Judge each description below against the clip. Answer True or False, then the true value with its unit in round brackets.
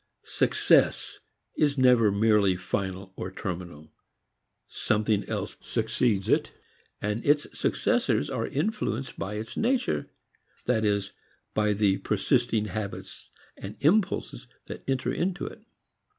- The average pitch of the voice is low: True (105 Hz)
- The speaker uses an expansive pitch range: False (4.9 semitones)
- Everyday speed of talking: False (115 wpm)